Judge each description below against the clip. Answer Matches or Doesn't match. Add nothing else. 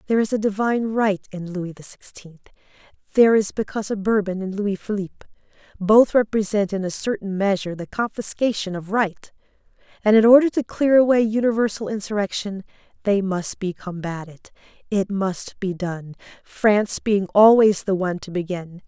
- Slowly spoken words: Doesn't match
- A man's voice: Doesn't match